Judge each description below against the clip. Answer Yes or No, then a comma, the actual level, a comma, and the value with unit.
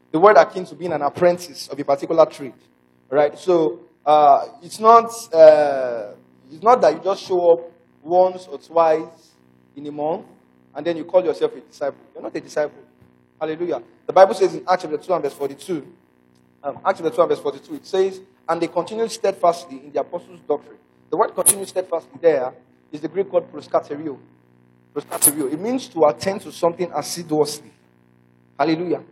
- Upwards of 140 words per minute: Yes, average, 180 wpm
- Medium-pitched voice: Yes, medium, 160 Hz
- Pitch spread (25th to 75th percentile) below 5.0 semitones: No, wide, 5.4 semitones